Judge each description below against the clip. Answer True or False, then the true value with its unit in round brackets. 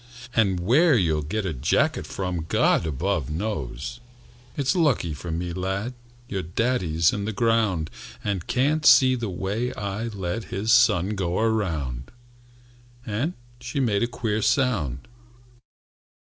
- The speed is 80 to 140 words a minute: True (135 wpm)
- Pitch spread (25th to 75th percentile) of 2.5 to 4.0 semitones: False (5.5 semitones)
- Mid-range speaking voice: False (100 Hz)